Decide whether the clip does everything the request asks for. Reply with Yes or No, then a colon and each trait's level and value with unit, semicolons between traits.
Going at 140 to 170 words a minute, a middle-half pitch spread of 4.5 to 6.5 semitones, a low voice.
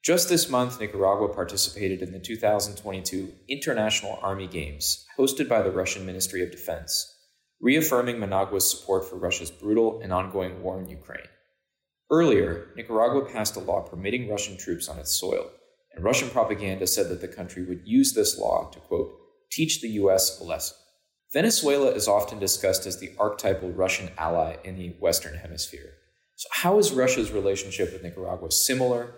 Yes: average, 160 wpm; average, 5.3 semitones; low, 100 Hz